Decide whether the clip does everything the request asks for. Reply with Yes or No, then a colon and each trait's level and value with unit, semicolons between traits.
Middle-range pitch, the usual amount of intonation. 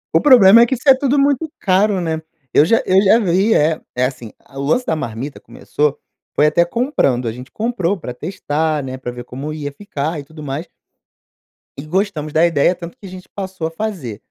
No: medium, 165 Hz; wide, 6.1 semitones